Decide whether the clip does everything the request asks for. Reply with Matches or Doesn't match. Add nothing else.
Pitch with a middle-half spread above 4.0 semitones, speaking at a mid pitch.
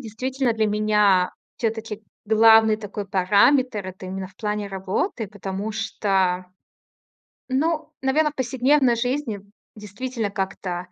Doesn't match